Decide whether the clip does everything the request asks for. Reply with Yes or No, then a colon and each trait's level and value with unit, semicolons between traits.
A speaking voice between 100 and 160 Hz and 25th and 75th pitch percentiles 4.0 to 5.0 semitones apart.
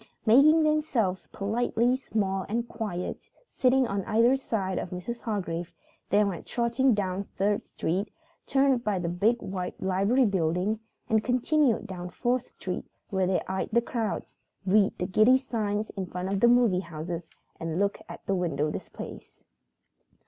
No: high, 205 Hz; average, 4.4 semitones